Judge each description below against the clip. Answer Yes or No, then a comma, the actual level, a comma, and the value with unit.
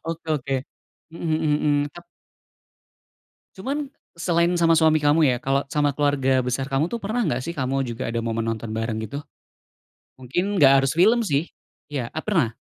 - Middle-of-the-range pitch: Yes, medium, 145 Hz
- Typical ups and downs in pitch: Yes, average, 4.7 semitones